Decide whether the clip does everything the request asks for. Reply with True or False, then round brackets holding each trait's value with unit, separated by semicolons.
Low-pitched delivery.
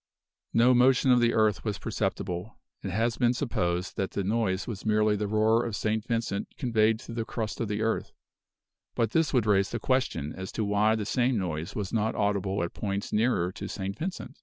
True (110 Hz)